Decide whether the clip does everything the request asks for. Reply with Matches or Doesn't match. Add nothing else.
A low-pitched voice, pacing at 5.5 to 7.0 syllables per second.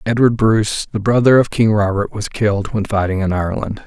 Matches